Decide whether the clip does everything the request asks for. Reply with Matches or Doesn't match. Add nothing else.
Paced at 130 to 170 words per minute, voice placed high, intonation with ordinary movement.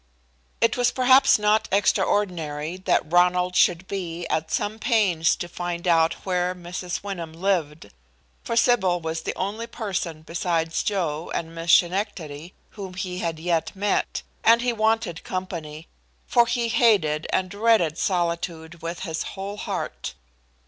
Doesn't match